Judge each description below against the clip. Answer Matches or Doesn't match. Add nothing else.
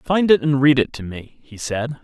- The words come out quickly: Matches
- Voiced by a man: Matches